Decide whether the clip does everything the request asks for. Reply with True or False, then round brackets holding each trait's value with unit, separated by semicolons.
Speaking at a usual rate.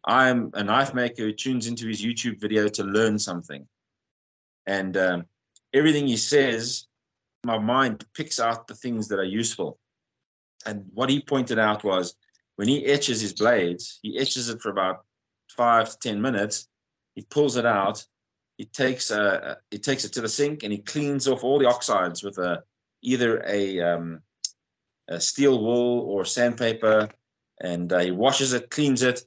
True (170 wpm)